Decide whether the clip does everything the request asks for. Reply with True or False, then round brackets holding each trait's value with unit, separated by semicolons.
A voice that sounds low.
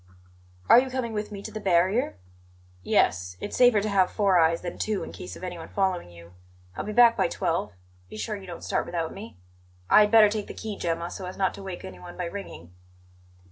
False (190 Hz)